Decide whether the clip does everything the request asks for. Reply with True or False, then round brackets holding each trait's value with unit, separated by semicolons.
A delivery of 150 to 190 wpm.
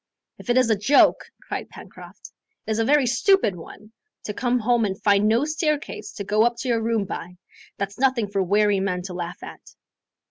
False (205 wpm)